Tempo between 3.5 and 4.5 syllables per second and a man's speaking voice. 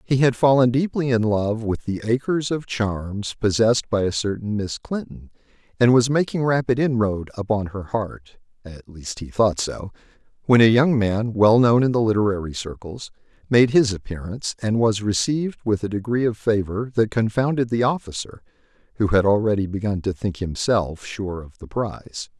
No: 4.9 syllables/s; male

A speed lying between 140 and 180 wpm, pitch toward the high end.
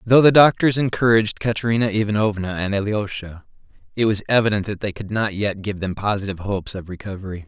No: average, 175 wpm; low, 105 Hz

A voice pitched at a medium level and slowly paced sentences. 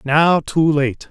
No: medium, 150 Hz; average, 160 wpm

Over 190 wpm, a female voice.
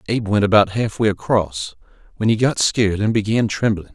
No: average, 200 wpm; male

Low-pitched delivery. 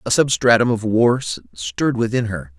Yes: low, 110 Hz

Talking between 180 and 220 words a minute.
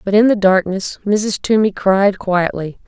No: average, 165 wpm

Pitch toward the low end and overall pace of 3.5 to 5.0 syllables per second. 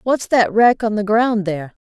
No: high, 215 Hz; 4.8 syllables/s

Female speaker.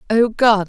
Yes: female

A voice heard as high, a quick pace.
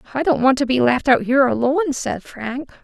Yes: very high, 265 Hz; fast, 235 wpm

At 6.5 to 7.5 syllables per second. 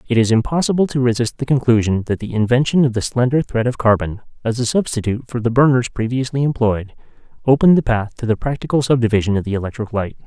Yes: 6.6 syllables/s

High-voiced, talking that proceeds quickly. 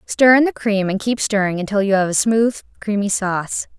Yes: high, 210 Hz; fast, 220 wpm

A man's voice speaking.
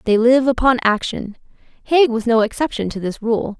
No: female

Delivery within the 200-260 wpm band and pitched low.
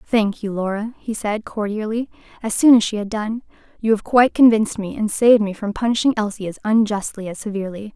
No: fast, 205 wpm; high, 215 Hz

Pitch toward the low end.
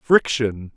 Yes: low, 120 Hz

